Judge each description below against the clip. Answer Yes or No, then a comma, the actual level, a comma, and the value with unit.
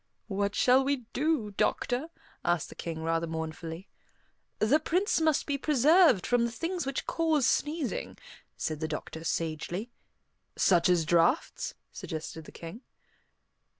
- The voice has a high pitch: Yes, high, 225 Hz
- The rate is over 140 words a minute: No, slow, 135 wpm